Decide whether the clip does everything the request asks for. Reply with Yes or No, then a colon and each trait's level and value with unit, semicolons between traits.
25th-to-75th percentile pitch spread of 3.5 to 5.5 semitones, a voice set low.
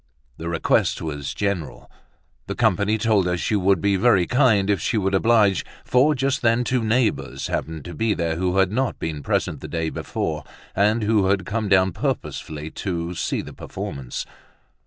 Yes: average, 4.8 semitones; low, 100 Hz